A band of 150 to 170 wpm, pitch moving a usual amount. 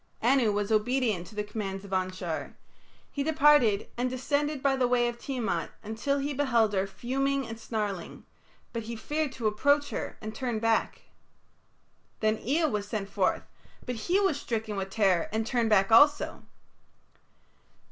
Yes: average, 160 wpm; average, 4.6 semitones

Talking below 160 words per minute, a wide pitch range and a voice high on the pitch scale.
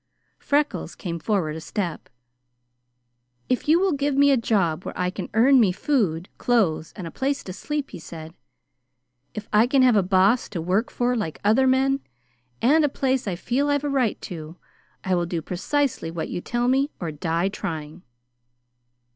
No: average, 180 wpm; wide, 7.6 semitones; high, 215 Hz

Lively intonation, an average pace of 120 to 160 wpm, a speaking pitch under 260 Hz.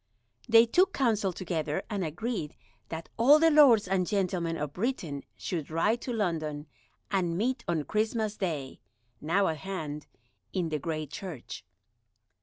Yes: wide, 5.8 semitones; average, 145 wpm; medium, 185 Hz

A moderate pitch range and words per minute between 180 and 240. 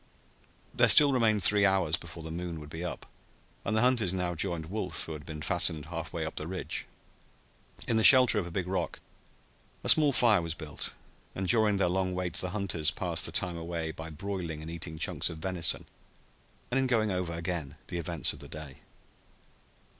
Yes: average, 3.4 semitones; average, 200 wpm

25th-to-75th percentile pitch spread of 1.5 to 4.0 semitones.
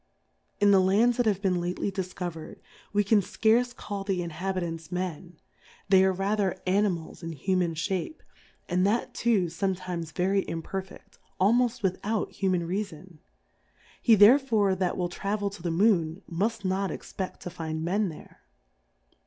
Yes: average, 2.7 semitones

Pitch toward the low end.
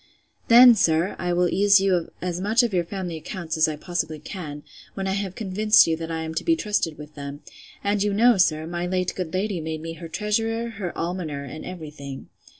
No: medium, 180 Hz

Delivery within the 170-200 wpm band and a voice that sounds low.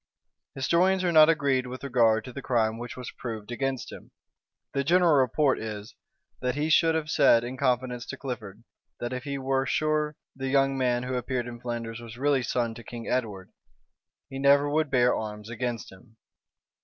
Yes: average, 185 wpm; low, 125 Hz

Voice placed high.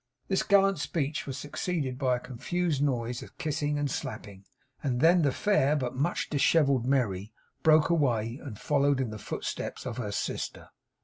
No: medium, 140 Hz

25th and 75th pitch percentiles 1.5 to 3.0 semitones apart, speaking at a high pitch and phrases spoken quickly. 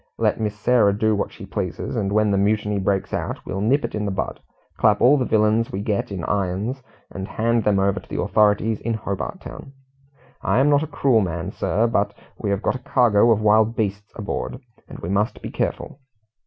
No: narrow, 2.5 semitones; low, 105 Hz; fast, 220 wpm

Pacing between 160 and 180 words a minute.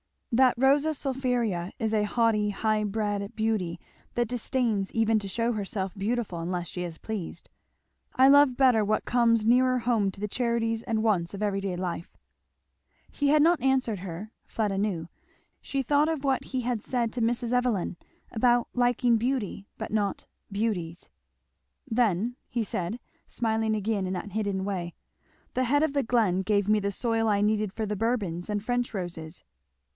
Yes: average, 170 wpm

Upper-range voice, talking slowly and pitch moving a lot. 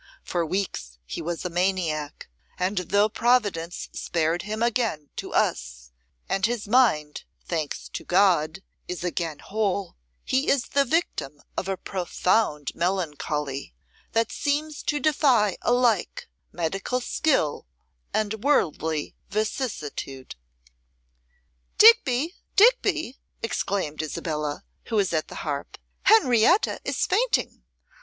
Yes: high, 195 Hz; slow, 115 wpm; wide, 7.6 semitones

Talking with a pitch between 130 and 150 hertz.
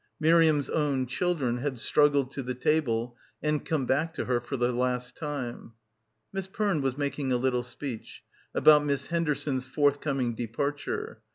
Yes: medium, 140 Hz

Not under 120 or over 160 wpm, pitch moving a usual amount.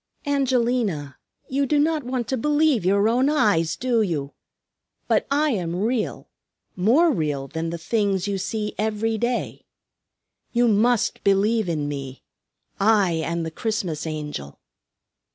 No: slow, 135 wpm; wide, 6.7 semitones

